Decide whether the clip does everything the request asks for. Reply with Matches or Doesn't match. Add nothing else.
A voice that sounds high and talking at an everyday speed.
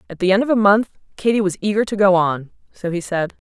Doesn't match